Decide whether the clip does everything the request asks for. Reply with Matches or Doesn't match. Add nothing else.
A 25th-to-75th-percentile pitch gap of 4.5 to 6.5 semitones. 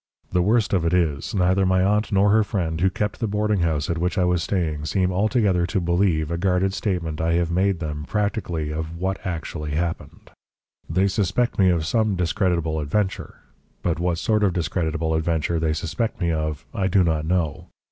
Doesn't match